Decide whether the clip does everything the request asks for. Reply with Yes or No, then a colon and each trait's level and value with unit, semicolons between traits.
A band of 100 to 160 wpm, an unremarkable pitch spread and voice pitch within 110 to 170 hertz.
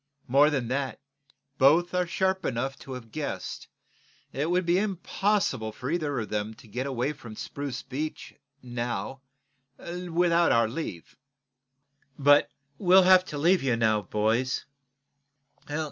No: average, 140 wpm; wide, 6.3 semitones; medium, 140 Hz